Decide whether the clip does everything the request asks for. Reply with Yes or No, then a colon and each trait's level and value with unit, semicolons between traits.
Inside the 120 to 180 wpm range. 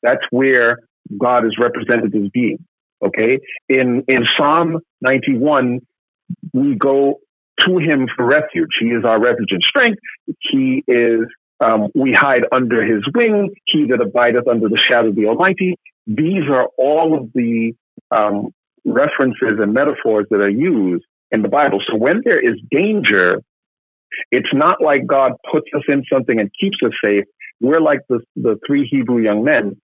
Yes: average, 165 wpm